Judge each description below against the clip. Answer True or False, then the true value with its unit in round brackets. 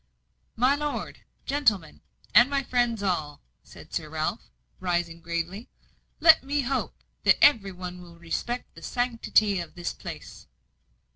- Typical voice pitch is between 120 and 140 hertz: False (205 Hz)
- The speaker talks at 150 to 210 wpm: False (135 wpm)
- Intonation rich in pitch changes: True (6.6 semitones)